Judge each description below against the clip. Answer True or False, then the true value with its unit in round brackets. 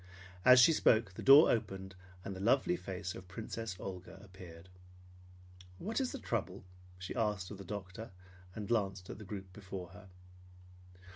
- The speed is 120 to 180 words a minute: True (160 wpm)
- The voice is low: True (100 Hz)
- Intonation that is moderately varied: True (3.4 semitones)